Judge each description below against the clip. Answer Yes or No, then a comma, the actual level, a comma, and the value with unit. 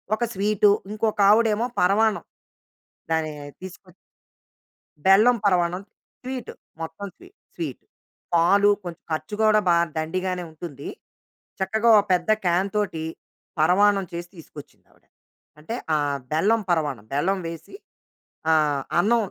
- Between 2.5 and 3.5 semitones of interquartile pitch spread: No, average, 4.5 semitones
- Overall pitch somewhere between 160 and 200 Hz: Yes, medium, 185 Hz